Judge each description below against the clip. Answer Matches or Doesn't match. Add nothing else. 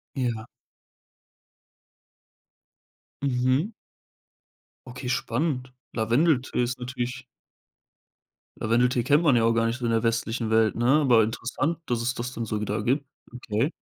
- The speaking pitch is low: Matches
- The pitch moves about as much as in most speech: Doesn't match